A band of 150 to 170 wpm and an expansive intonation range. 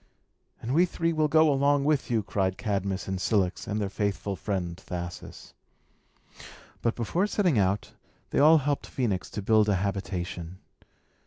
Yes: average, 155 wpm; wide, 7.0 semitones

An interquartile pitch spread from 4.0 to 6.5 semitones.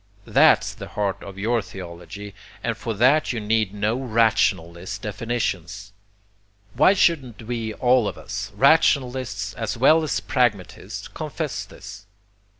No: average, 3.5 semitones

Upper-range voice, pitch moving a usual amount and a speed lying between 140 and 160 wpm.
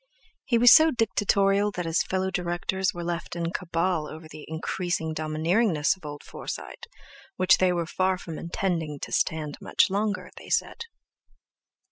No: medium, 175 Hz; average, 3.1 semitones; average, 155 wpm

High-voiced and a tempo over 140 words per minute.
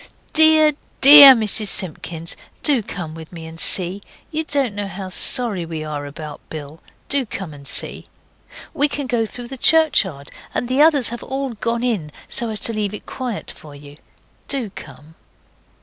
Yes: high, 210 Hz; average, 175 wpm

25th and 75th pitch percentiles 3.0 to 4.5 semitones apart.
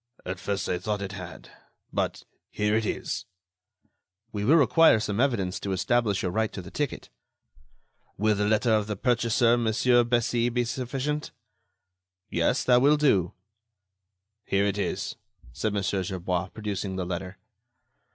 Yes: average, 3.9 semitones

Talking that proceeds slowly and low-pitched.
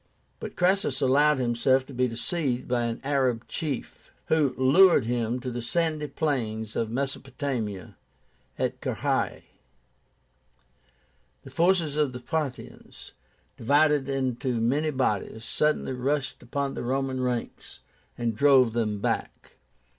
Yes: slow, 125 wpm; low, 130 Hz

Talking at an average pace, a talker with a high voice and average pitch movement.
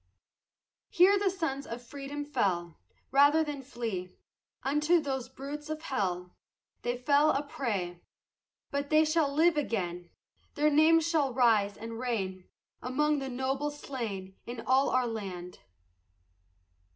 No: slow, 125 wpm; very high, 270 Hz; average, 5.0 semitones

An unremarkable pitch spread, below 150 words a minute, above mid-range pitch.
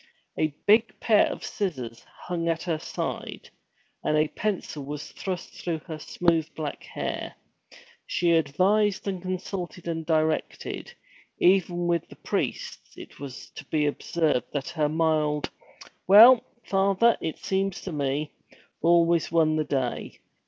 No: average, 3.4 semitones; average, 140 wpm; medium, 165 Hz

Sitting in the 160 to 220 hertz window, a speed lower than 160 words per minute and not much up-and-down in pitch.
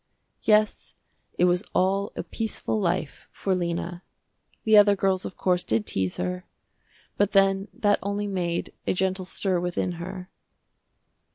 Yes: medium, 185 Hz; average, 145 wpm; narrow, 2.3 semitones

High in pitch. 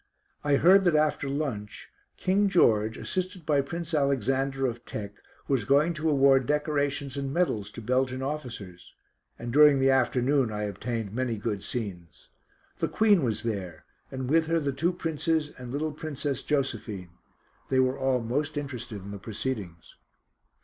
No: low, 135 Hz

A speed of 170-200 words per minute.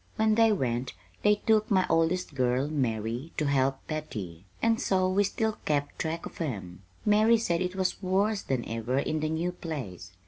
Yes: average, 180 wpm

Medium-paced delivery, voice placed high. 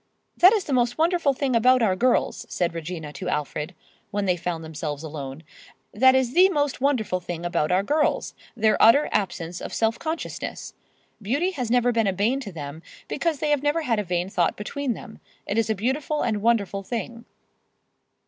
Yes: average, 190 wpm; high, 225 Hz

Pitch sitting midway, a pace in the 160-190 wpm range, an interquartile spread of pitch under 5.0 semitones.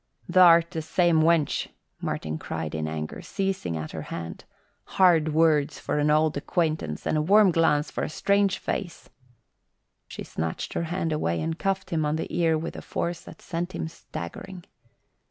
Yes: medium, 160 Hz; average, 170 wpm; average, 2.9 semitones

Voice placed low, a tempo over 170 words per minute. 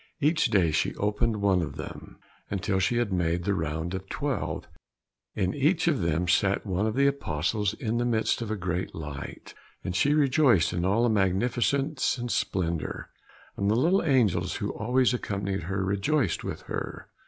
Yes: low, 100 Hz; average, 180 wpm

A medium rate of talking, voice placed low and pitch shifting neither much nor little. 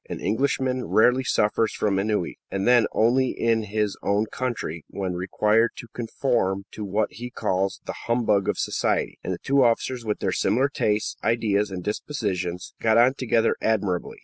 Yes: average, 170 wpm; low, 110 Hz; average, 3.5 semitones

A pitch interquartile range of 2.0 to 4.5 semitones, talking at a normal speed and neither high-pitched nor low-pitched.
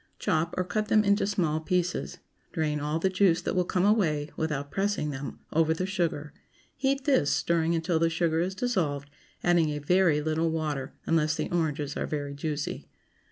Yes: average, 3.5 semitones; average, 180 wpm; medium, 165 Hz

